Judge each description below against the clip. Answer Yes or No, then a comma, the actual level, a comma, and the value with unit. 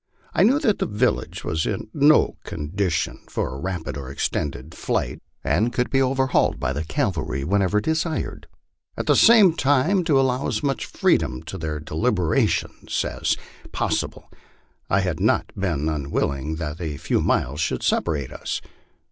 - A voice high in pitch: No, very low, 95 Hz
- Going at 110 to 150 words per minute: No, average, 160 wpm